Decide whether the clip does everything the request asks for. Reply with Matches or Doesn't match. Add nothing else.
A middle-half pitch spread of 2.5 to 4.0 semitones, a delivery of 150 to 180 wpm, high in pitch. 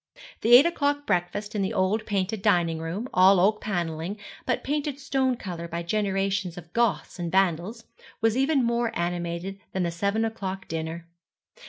Doesn't match